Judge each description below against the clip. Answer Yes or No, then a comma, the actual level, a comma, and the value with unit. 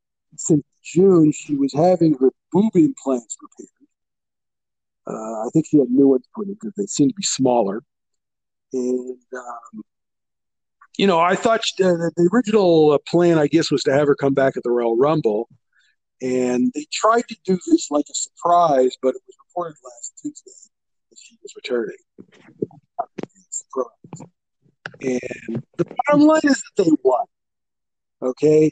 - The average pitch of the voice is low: No, medium, 160 Hz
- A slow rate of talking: No, average, 155 wpm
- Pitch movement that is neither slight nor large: No, wide, 7.4 semitones